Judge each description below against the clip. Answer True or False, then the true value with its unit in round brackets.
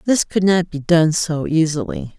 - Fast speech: False (190 wpm)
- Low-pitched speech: False (165 Hz)